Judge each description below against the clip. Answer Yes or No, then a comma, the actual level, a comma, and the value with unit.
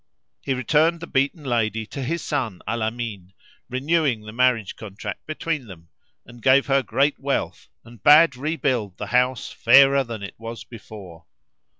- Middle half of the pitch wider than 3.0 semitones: Yes, average, 4.1 semitones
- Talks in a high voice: No, low, 125 Hz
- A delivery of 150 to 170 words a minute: Yes, average, 160 wpm